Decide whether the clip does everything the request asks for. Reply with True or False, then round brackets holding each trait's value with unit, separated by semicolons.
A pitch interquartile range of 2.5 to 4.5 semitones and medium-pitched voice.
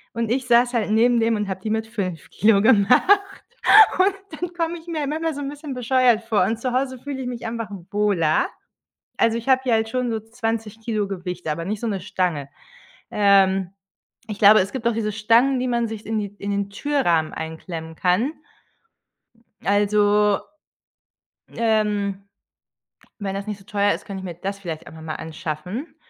False (3.6 semitones; 215 Hz)